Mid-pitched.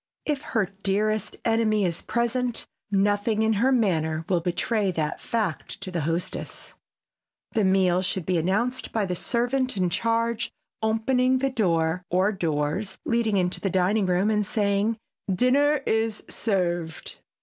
No: high, 205 Hz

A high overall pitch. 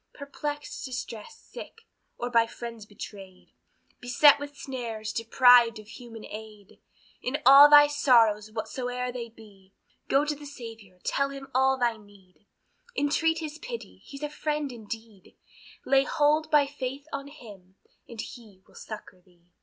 Yes: high, 245 Hz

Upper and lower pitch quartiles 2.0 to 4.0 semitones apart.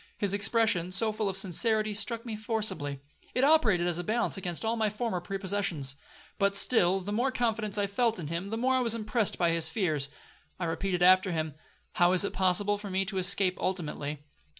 Yes: average, 3.7 semitones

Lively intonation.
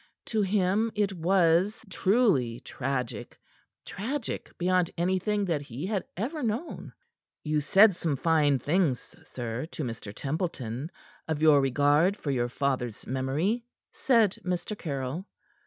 Yes: wide, 6.4 semitones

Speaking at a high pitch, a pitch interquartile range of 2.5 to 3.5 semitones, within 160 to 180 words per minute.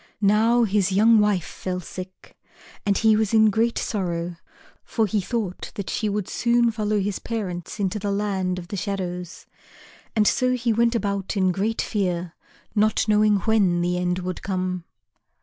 Yes: high, 200 Hz; average, 3.0 semitones; average, 165 wpm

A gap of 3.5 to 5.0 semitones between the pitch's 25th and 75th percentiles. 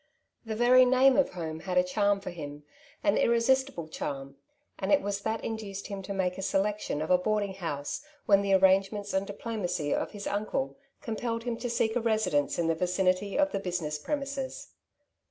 Yes: average, 4.0 semitones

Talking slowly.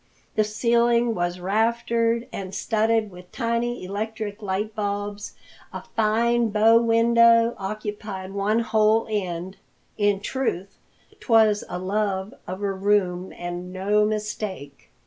Yes: slow, 120 wpm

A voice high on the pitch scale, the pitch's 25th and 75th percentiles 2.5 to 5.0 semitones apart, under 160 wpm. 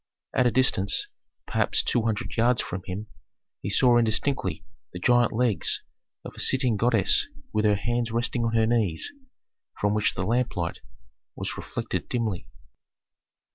No: low, 115 Hz; average, 2.9 semitones; average, 145 wpm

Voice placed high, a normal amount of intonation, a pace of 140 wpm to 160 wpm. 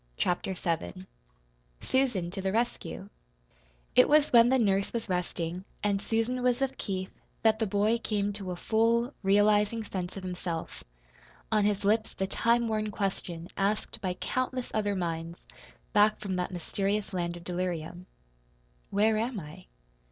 Yes: high, 200 Hz; average, 3.5 semitones; average, 150 wpm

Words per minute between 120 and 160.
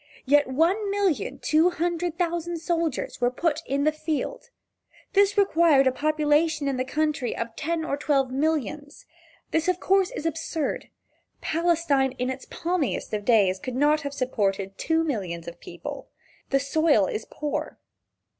Yes: average, 150 wpm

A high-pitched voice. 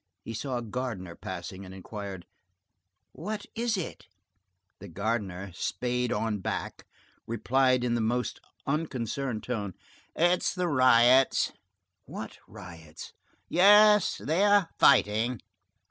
No: low, 120 Hz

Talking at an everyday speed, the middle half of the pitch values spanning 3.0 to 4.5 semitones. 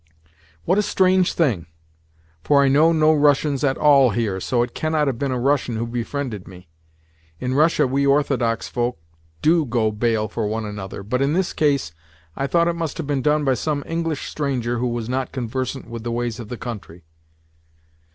Yes: average, 190 wpm; average, 4.2 semitones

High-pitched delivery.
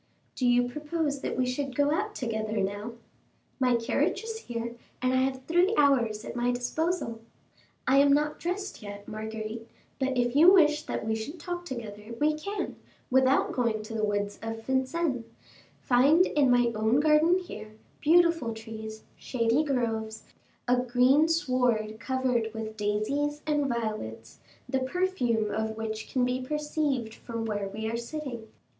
Yes: very high, 250 Hz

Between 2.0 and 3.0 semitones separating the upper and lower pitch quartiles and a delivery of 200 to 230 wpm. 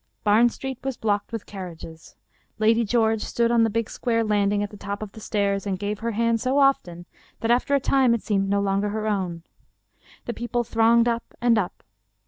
Yes: narrow, 2.6 semitones; fast, 205 wpm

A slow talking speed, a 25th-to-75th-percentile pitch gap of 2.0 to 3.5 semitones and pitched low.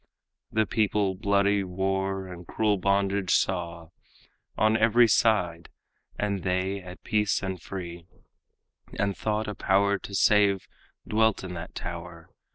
Yes: slow, 130 wpm; narrow, 2.4 semitones; very low, 95 Hz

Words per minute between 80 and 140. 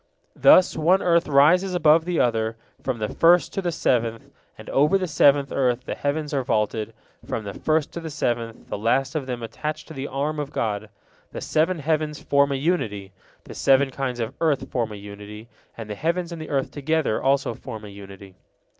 No: average, 200 wpm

